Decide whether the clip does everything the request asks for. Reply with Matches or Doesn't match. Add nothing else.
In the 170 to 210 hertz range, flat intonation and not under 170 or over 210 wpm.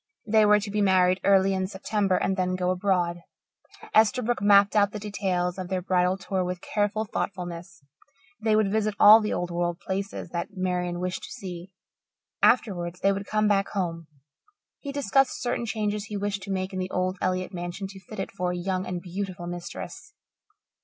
Matches